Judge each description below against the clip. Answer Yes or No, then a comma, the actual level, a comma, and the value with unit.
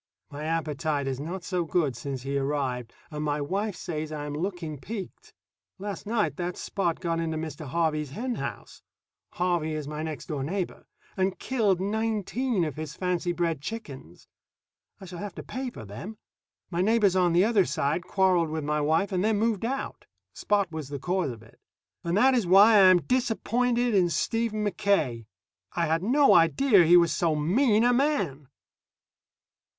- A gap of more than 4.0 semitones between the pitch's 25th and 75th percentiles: Yes, average, 5.3 semitones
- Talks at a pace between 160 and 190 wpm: Yes, average, 175 wpm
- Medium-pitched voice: Yes, medium, 175 Hz